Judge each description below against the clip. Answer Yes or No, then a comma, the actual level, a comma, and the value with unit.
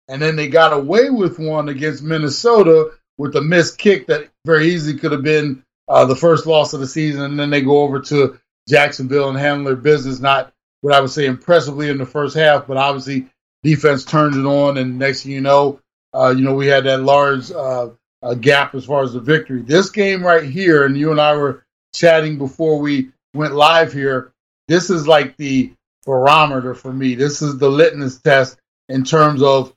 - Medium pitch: Yes, medium, 145 Hz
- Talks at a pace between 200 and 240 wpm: Yes, fast, 205 wpm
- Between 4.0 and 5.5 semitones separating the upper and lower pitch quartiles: No, narrow, 2.4 semitones